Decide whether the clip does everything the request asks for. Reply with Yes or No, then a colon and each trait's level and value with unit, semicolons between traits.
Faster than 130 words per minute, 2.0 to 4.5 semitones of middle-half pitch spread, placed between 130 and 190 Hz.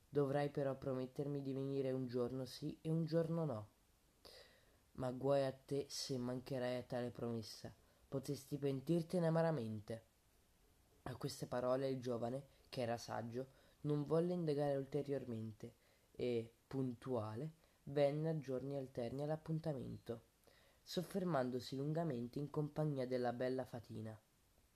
No: average, 120 wpm; average, 3.1 semitones; low, 135 Hz